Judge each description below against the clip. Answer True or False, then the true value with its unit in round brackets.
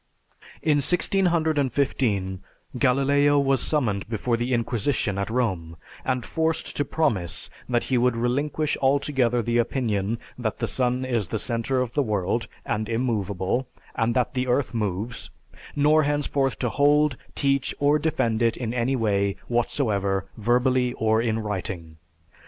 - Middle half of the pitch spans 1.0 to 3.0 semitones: False (4.1 semitones)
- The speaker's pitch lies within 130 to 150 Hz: False (120 Hz)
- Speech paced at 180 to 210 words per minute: False (140 wpm)